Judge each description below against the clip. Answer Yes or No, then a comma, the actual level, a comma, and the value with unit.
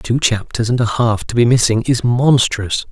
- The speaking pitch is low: Yes, low, 115 Hz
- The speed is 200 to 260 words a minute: Yes, fast, 205 wpm